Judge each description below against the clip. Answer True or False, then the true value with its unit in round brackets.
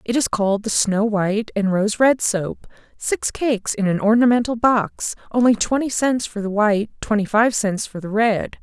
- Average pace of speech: True (195 wpm)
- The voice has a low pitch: False (220 Hz)